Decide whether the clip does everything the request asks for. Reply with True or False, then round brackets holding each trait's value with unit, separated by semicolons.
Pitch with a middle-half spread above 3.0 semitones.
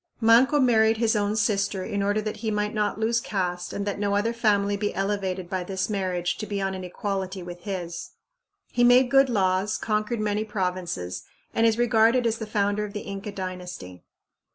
False (2.7 semitones)